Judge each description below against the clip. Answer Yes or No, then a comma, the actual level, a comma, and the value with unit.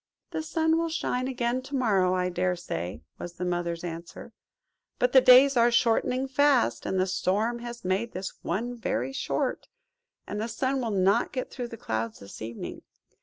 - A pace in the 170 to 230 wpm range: Yes, average, 180 wpm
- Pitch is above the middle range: Yes, high, 230 Hz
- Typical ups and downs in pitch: No, wide, 5.8 semitones